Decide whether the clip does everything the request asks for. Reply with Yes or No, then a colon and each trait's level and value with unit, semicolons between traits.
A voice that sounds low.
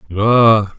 Yes: low, 105 Hz